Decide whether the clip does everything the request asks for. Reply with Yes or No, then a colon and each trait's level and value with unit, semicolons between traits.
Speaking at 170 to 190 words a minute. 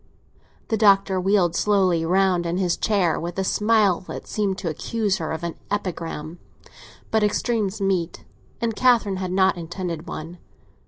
No: average, 155 wpm